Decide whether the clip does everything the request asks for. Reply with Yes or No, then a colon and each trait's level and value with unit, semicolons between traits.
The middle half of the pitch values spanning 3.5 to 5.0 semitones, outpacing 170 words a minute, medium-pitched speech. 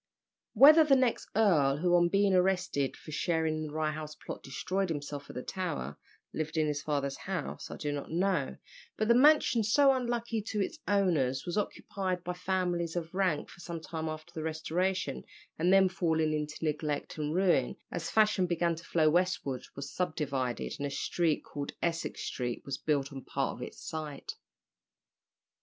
Yes: average, 4.1 semitones; average, 180 wpm; medium, 165 Hz